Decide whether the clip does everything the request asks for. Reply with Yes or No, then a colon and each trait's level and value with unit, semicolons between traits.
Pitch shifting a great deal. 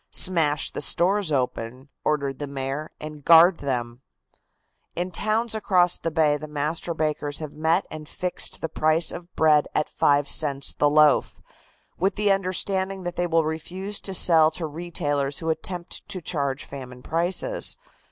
No: average, 3.5 semitones